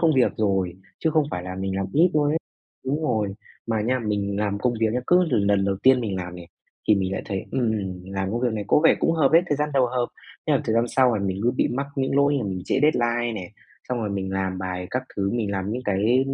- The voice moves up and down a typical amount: Yes, average, 5.0 semitones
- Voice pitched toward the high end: No, low, 110 Hz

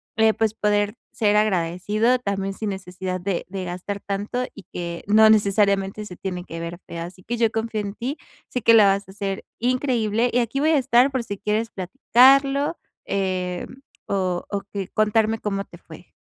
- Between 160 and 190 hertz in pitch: No, high, 205 Hz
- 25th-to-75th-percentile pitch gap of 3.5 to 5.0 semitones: No, average, 3.0 semitones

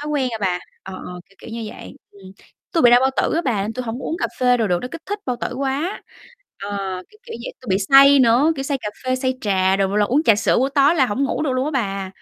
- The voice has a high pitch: Yes, very high, 250 Hz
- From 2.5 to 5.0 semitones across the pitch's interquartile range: No, wide, 5.4 semitones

